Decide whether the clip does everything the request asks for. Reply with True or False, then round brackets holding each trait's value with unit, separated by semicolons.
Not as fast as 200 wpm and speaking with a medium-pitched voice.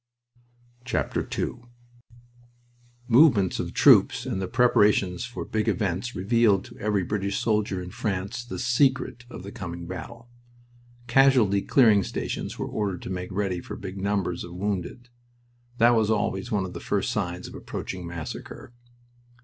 False (150 wpm; 100 Hz)